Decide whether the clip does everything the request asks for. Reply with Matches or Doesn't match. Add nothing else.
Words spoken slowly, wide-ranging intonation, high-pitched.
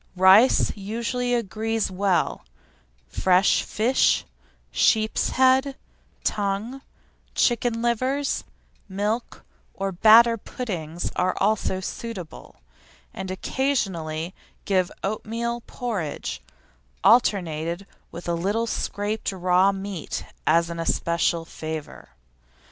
Doesn't match